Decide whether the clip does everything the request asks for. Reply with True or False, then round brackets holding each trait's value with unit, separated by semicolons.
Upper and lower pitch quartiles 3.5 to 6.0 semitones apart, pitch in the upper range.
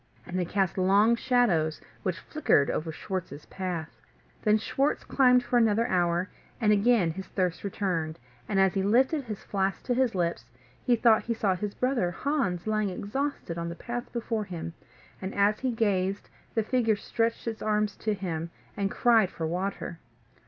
True (4.3 semitones; 200 Hz)